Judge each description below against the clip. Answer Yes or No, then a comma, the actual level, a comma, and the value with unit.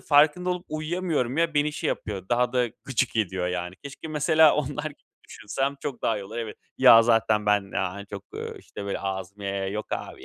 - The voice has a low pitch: Yes, low, 120 Hz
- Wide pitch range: Yes, wide, 6.7 semitones